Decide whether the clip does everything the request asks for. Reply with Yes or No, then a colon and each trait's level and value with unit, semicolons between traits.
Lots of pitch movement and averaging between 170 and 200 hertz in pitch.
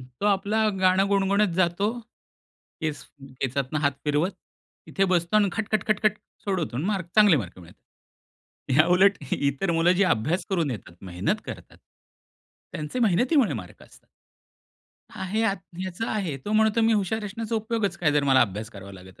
Yes: wide, 6.6 semitones; medium, 185 Hz